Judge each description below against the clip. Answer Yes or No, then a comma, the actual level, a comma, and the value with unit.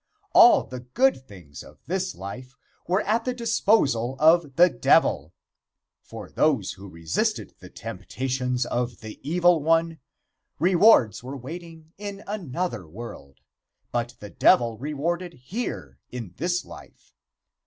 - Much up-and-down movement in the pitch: Yes, wide, 6.9 semitones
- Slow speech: Yes, slow, 130 wpm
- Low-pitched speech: No, medium, 145 Hz